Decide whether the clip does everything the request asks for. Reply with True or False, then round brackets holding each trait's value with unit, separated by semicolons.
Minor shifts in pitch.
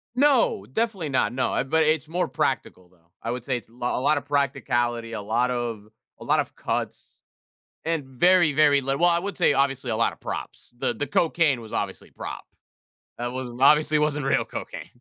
False (4.3 semitones)